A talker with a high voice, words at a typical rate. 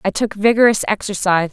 Yes: high, 205 Hz; average, 160 wpm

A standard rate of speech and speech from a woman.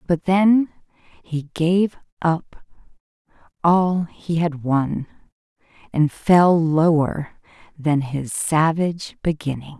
No: slow, 100 wpm; female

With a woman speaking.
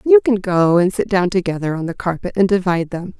Yes: female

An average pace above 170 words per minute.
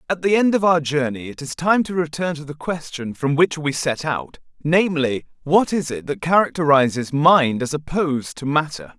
Yes: average, 200 wpm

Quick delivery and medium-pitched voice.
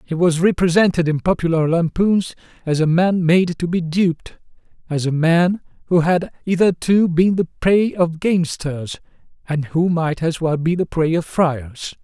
No: average, 170 wpm; medium, 170 Hz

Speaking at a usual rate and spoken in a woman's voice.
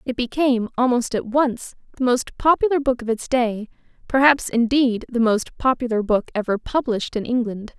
Yes: average, 170 wpm; female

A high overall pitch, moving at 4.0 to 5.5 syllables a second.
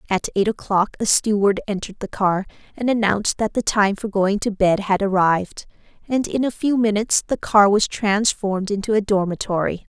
Yes: high, 205 Hz; 5.3 syllables/s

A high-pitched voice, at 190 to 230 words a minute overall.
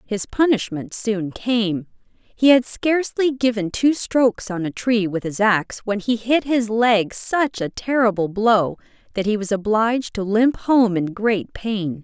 No: high, 220 Hz; average, 175 wpm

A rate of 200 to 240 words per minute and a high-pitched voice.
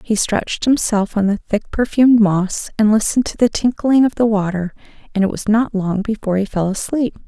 Yes: fast, 205 wpm; high, 215 Hz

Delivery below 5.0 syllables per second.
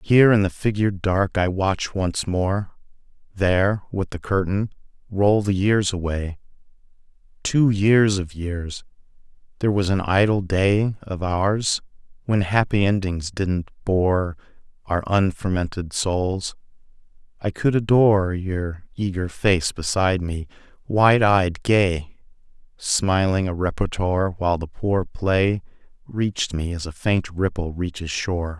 Yes: 4.0 syllables/s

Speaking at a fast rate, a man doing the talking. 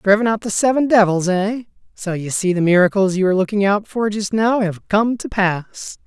Yes: fast, 220 wpm; male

